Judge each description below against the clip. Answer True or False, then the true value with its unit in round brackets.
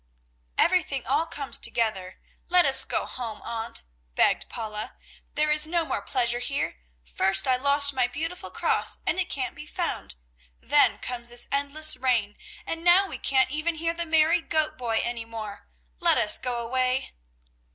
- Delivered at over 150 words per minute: True (165 wpm)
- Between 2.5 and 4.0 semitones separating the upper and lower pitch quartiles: False (4.9 semitones)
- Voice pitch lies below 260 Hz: False (265 Hz)